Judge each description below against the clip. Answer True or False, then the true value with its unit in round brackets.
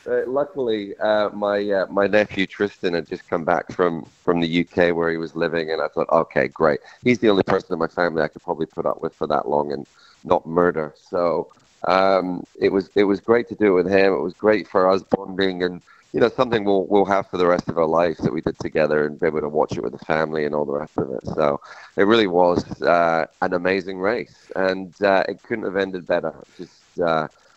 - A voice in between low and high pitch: False (95 Hz)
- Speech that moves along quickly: True (240 wpm)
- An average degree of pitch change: True (3.0 semitones)